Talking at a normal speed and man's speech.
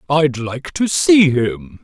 Yes: average, 165 wpm; male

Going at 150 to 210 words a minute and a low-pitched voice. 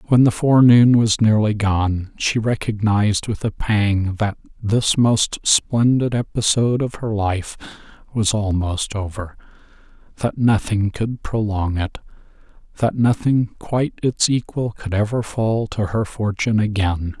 No: slow, 135 wpm; low, 110 Hz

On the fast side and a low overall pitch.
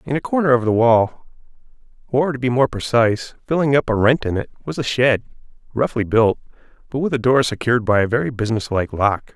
Yes: fast, 210 wpm; low, 120 Hz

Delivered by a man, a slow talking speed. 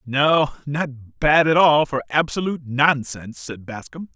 Yes: male; slow, 130 wpm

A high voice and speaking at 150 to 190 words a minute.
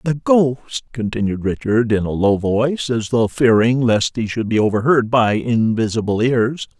No: low, 115 Hz; average, 170 wpm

